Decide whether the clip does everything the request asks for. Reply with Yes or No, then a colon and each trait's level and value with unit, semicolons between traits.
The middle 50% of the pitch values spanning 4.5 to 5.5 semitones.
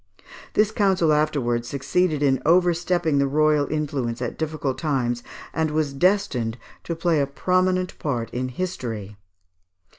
Yes: average, 5.2 semitones